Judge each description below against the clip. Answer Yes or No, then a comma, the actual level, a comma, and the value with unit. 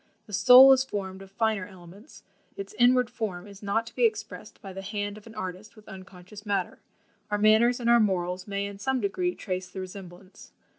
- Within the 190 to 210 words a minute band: Yes, average, 200 wpm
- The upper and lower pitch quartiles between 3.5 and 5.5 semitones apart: No, average, 3.0 semitones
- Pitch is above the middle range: Yes, high, 205 Hz